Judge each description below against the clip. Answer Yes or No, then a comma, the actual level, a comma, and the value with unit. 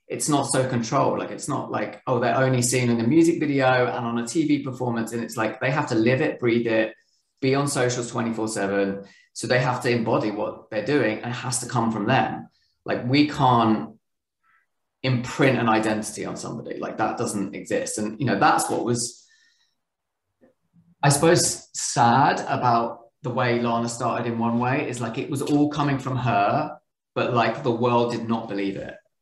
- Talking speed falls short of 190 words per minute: No, average, 195 wpm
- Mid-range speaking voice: No, low, 120 Hz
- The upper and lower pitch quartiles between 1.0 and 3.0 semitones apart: Yes, narrow, 2.6 semitones